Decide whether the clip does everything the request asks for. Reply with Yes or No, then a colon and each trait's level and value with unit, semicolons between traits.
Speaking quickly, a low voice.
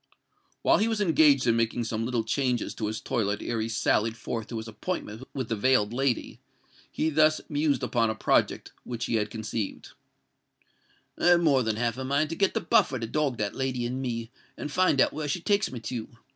Yes: fast, 215 wpm; low, 125 Hz